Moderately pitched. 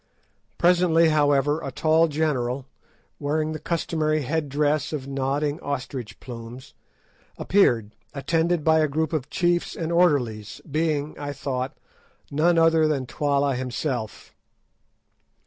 Yes: medium, 150 Hz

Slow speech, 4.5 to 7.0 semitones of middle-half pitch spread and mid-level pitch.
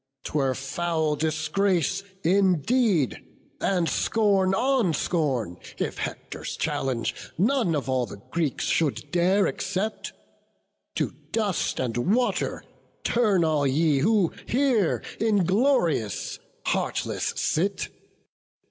Yes: slow, 100 wpm; wide, 5.6 semitones; medium, 175 Hz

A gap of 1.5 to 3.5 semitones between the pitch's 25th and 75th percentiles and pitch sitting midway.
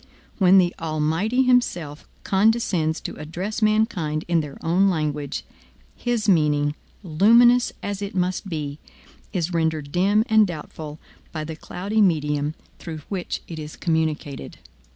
No: average, 4.8 semitones; medium, 170 Hz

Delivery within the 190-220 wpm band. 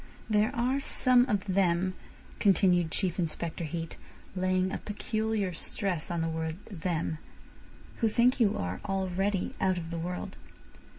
No: average, 140 wpm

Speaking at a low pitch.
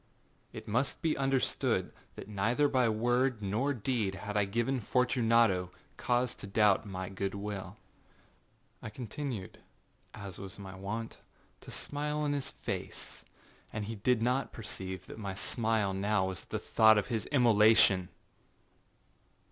Yes: low, 110 Hz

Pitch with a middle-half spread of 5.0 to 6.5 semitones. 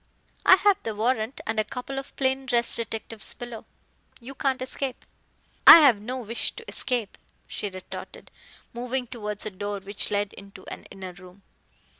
No: average, 4.1 semitones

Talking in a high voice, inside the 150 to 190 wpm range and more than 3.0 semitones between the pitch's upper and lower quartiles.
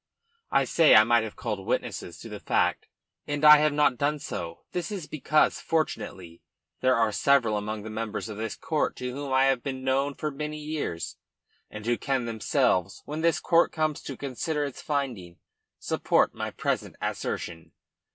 No: low, 135 Hz; average, 180 wpm; wide, 5.5 semitones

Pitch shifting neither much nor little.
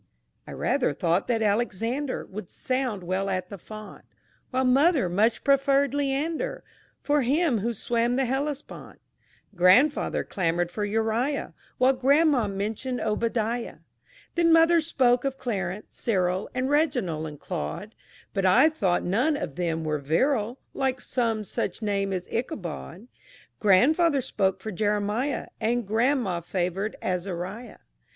No: wide, 5.9 semitones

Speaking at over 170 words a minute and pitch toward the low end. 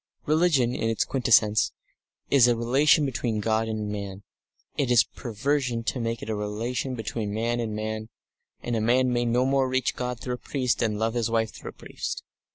Yes: average, 195 wpm; low, 115 Hz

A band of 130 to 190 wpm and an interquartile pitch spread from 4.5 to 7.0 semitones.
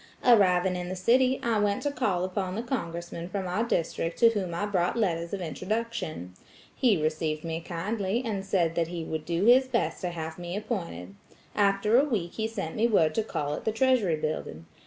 No: average, 200 wpm; average, 4.9 semitones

